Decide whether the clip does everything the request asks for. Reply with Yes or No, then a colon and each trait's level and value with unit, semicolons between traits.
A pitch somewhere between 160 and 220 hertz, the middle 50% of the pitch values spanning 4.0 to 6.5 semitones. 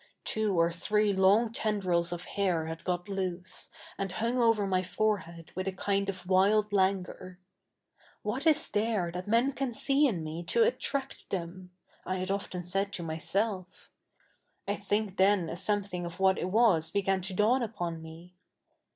No: high, 190 Hz; average, 3.0 semitones